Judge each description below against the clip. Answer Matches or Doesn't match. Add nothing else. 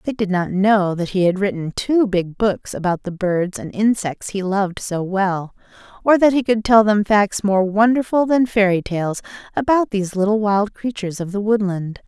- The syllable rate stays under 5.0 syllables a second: Matches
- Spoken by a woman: Matches